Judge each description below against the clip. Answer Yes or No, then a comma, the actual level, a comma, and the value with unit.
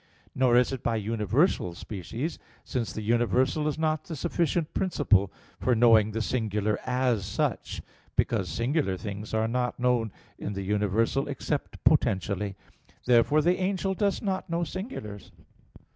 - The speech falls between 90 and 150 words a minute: Yes, average, 145 wpm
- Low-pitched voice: Yes, low, 120 Hz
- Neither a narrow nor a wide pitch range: No, wide, 6.3 semitones